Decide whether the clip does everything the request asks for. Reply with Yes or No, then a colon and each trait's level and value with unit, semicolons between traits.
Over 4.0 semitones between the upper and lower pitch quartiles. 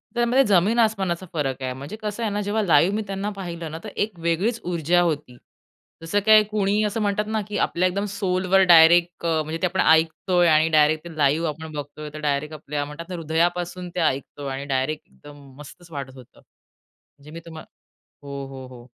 Yes: average, 4.5 semitones